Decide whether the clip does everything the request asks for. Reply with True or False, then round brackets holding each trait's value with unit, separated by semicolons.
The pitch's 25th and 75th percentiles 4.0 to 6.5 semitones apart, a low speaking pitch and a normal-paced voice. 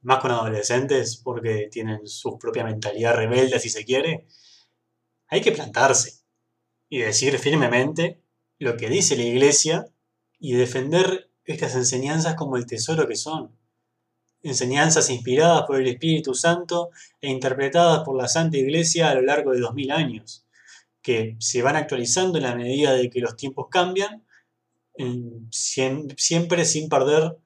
True (5.1 semitones; 130 Hz; 140 wpm)